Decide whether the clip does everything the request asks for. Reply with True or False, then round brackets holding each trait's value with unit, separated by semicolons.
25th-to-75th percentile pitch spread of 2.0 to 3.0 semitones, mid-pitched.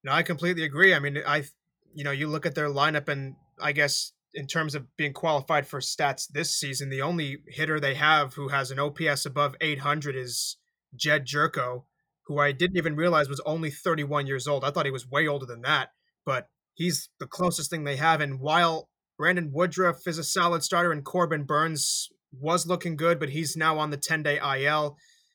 True (2.7 semitones; 150 Hz)